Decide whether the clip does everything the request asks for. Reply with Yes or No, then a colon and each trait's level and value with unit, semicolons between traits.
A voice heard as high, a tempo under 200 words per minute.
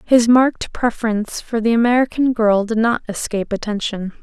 Yes: high, 225 Hz; average, 155 wpm